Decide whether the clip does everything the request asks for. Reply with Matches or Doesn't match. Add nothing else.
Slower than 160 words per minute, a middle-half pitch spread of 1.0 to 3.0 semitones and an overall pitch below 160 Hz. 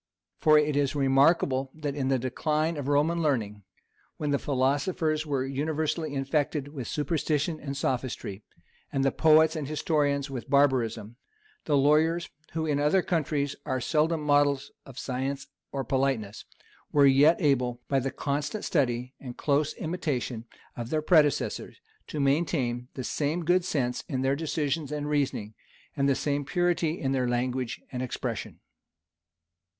Matches